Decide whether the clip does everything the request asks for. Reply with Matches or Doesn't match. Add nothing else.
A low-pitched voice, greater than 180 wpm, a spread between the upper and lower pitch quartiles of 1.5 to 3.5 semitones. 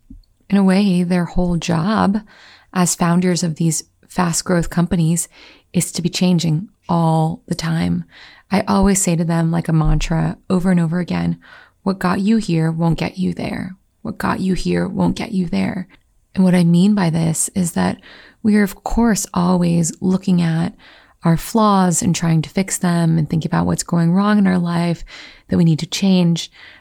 Doesn't match